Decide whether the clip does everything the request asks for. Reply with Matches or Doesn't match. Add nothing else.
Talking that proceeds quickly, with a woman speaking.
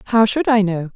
Matches